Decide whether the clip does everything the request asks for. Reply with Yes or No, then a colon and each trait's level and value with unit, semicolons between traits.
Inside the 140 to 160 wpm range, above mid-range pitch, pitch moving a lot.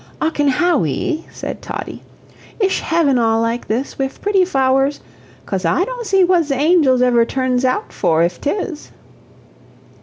Yes: average, 150 wpm; very high, 275 Hz; wide, 6.3 semitones